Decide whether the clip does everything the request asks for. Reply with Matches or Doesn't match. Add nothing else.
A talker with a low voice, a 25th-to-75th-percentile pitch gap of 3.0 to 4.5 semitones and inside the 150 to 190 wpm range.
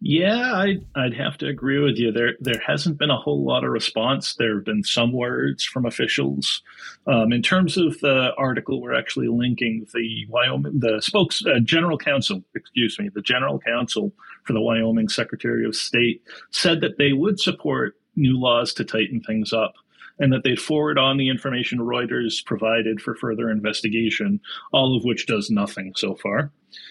Matches